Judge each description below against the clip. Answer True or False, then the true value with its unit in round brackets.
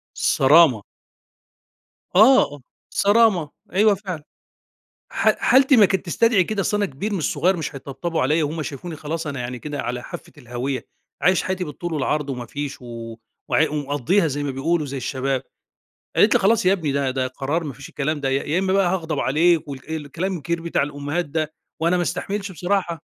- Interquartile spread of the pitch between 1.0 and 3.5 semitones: False (4.7 semitones)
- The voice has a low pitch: False (155 Hz)